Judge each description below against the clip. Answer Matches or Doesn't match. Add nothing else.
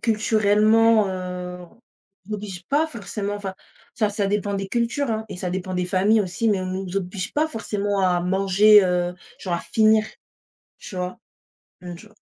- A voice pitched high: Matches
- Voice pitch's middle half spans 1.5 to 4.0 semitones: Matches